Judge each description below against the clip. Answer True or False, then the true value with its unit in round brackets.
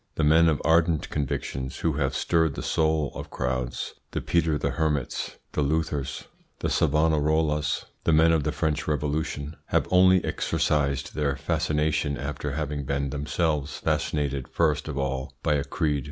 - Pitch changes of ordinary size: False (2.1 semitones)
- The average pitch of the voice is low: True (75 Hz)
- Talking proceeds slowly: False (155 wpm)